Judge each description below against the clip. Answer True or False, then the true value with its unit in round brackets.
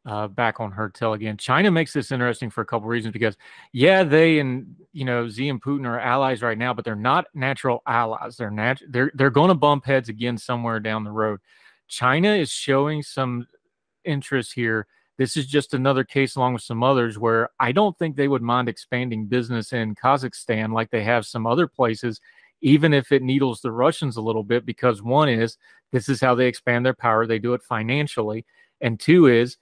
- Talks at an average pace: False (210 wpm)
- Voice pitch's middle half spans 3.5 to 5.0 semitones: False (3.0 semitones)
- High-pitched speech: False (125 Hz)